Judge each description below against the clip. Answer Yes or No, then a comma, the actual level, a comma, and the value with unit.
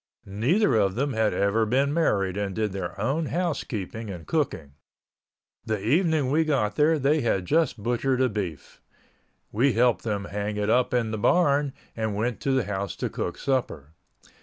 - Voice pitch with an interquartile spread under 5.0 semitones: No, wide, 5.4 semitones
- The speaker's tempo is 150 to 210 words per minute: Yes, average, 175 wpm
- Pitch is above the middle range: No, low, 115 Hz